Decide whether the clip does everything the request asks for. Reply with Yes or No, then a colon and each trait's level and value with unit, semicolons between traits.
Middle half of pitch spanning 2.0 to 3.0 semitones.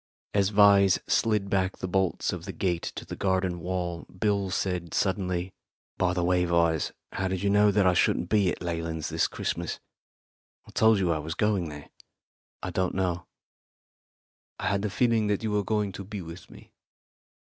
Yes: narrow, 2.5 semitones